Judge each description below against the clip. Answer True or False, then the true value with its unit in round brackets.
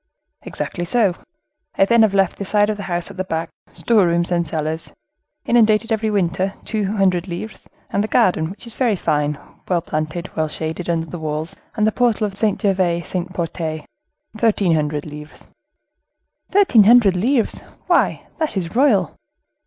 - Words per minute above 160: True (170 wpm)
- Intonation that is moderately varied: True (4.4 semitones)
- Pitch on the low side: False (185 Hz)